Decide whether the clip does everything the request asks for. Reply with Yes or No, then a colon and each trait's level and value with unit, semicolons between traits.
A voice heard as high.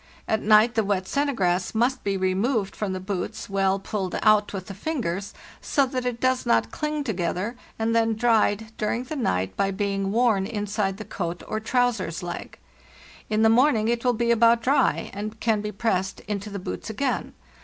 Yes: high, 215 Hz